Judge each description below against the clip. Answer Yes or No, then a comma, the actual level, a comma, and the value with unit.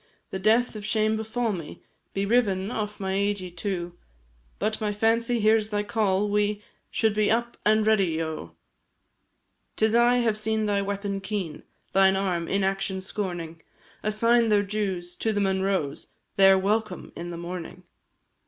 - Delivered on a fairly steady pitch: Yes, narrow, 2.3 semitones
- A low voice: No, high, 205 Hz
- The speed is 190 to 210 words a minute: No, average, 155 wpm